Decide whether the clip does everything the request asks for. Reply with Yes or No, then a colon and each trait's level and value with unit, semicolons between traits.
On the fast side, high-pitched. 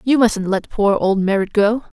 Yes: fast, 210 wpm; high, 210 Hz